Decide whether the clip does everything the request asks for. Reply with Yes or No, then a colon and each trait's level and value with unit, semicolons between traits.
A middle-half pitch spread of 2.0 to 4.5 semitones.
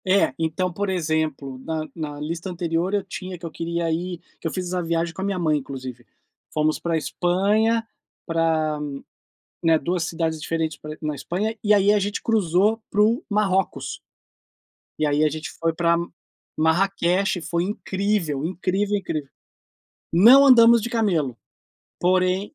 Yes: average, 3.7 semitones